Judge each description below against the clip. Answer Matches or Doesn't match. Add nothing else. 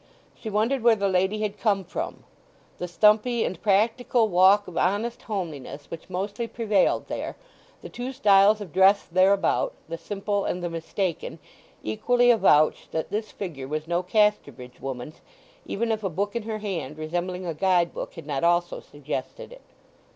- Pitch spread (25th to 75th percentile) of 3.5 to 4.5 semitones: Matches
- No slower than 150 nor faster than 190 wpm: Matches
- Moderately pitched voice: Doesn't match